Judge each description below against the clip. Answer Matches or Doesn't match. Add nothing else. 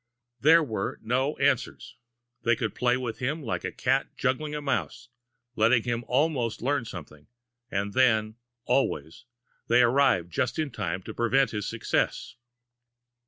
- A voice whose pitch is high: Doesn't match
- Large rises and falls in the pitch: Doesn't match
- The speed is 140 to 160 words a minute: Matches